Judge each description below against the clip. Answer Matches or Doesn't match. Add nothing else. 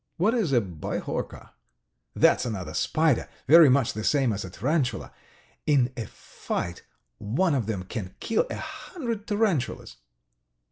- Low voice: Matches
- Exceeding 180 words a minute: Doesn't match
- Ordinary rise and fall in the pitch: Doesn't match